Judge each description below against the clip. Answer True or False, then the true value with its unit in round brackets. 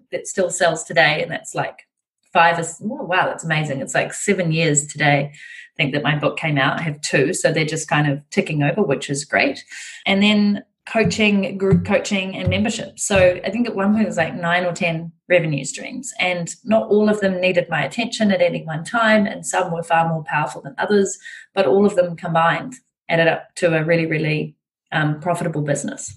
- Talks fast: True (215 wpm)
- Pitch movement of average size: True (4.3 semitones)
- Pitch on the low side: False (175 Hz)